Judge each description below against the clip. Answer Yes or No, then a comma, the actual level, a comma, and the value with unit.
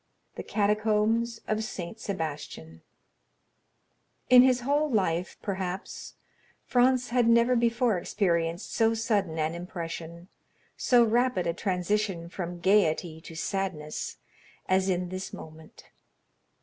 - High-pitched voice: Yes, high, 195 Hz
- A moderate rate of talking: No, slow, 110 wpm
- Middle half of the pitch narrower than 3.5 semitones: No, average, 5.1 semitones